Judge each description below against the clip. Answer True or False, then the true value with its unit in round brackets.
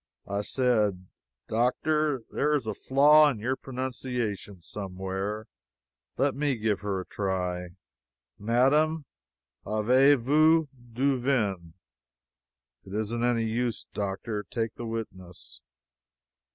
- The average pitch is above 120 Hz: False (115 Hz)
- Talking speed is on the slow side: True (100 wpm)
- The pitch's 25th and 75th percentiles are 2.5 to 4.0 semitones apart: False (4.7 semitones)